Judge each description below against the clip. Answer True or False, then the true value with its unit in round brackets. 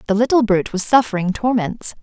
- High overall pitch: True (215 Hz)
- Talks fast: False (180 wpm)